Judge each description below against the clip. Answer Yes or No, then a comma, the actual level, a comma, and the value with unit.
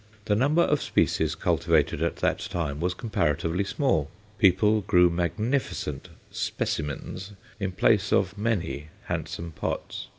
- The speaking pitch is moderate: No, very low, 95 Hz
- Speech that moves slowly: Yes, slow, 125 wpm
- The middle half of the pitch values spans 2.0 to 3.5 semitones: No, average, 4.4 semitones